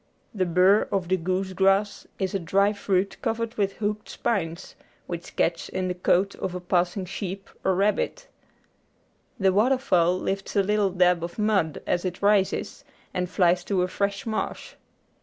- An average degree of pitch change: No, narrow, 2.0 semitones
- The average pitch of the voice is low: No, high, 190 Hz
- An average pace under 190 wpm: Yes, average, 170 wpm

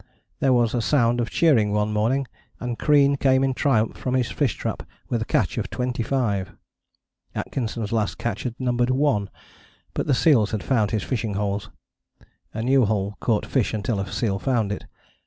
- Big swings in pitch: No, average, 3.6 semitones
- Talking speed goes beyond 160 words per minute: Yes, average, 180 wpm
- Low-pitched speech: Yes, low, 120 Hz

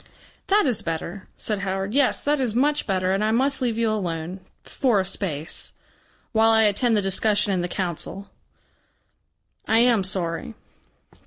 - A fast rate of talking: No, average, 160 wpm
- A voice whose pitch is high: Yes, high, 210 Hz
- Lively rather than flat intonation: No, average, 3.8 semitones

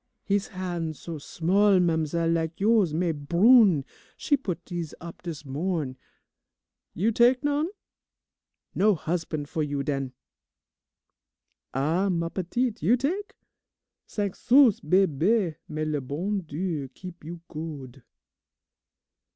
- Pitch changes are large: No, average, 4.7 semitones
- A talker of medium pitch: Yes, medium, 170 Hz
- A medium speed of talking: No, slow, 120 wpm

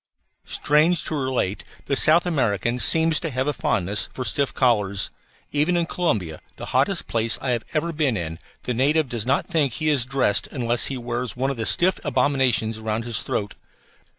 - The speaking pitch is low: Yes, low, 130 Hz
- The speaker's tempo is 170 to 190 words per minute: Yes, average, 185 wpm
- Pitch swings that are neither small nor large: Yes, average, 5.0 semitones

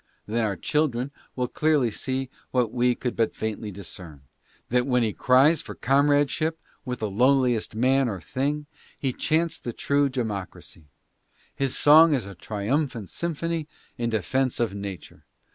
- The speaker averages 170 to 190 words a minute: No, average, 155 wpm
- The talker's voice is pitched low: Yes, low, 125 Hz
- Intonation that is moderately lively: Yes, average, 4.5 semitones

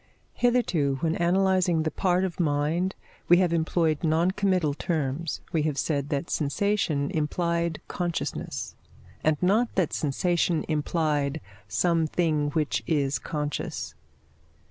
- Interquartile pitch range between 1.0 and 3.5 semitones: Yes, average, 3.0 semitones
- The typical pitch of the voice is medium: Yes, medium, 160 Hz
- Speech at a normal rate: No, slow, 120 wpm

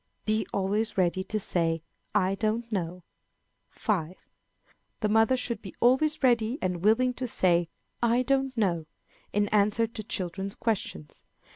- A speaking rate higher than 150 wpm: No, average, 140 wpm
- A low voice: No, high, 215 Hz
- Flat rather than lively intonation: No, average, 4.1 semitones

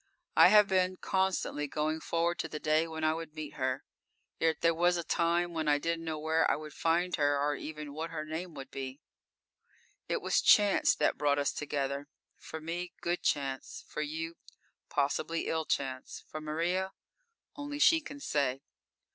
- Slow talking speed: No, average, 180 wpm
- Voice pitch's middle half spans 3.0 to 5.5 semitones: No, narrow, 2.6 semitones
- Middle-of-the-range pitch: Yes, medium, 160 Hz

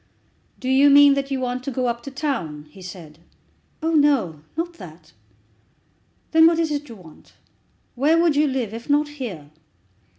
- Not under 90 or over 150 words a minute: No, average, 175 wpm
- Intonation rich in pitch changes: Yes, wide, 7.4 semitones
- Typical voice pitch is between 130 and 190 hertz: No, very high, 265 Hz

